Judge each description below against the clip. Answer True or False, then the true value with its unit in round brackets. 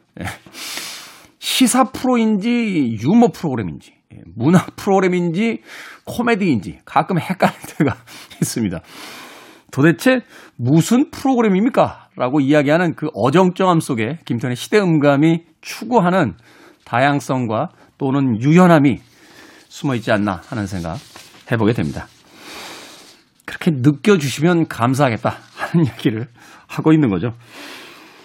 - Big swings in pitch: True (5.8 semitones)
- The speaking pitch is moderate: True (160 Hz)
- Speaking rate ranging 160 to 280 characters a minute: True (270 characters per minute)